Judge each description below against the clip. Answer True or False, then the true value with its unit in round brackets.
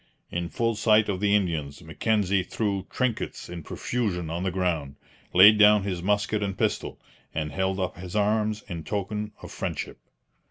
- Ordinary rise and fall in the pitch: True (3.2 semitones)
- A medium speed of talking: True (165 wpm)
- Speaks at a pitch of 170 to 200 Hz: False (95 Hz)